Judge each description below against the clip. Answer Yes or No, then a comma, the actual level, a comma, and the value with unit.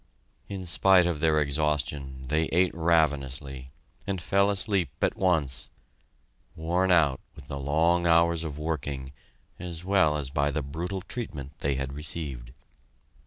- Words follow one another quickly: No, average, 140 wpm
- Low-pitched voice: Yes, very low, 80 Hz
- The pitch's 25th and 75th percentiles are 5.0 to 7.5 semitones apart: No, average, 3.8 semitones